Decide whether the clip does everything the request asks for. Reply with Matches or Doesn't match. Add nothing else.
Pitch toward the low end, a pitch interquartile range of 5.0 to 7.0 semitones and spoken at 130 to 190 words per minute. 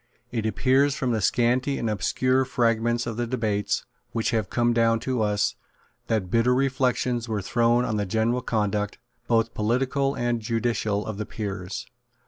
Doesn't match